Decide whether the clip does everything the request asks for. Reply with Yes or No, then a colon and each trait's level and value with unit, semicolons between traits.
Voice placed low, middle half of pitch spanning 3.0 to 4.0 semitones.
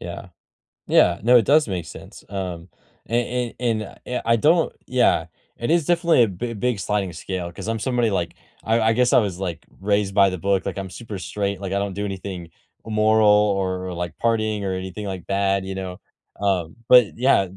Yes: low, 100 Hz; average, 3.5 semitones